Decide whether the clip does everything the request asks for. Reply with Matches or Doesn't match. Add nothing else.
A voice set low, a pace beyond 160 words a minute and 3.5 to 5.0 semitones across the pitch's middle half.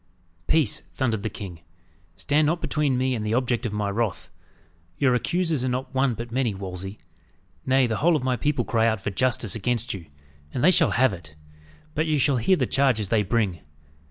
Matches